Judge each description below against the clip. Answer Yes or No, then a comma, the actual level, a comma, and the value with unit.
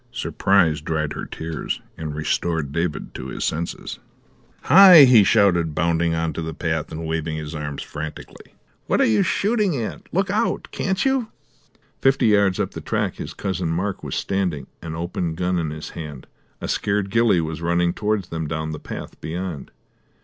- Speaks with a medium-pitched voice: No, very low, 85 Hz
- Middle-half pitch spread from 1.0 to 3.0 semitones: No, average, 4.1 semitones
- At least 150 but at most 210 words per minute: Yes, average, 175 wpm